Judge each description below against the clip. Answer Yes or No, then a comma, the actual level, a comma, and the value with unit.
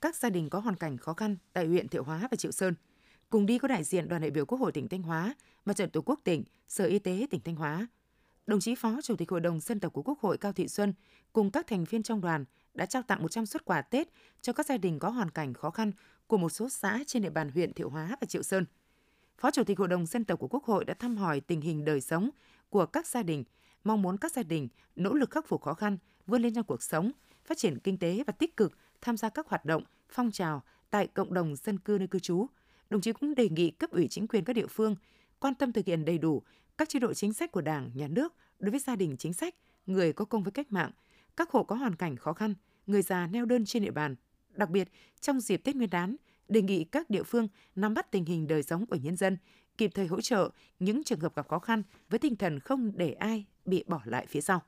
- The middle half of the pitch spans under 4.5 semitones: No, average, 5.3 semitones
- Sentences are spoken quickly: Yes, fast, 265 wpm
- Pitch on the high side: Yes, high, 200 Hz